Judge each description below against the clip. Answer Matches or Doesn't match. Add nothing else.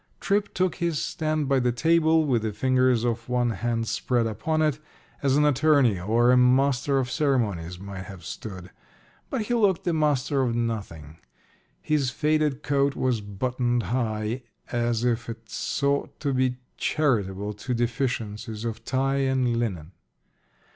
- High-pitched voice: Doesn't match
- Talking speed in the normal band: Matches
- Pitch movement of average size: Matches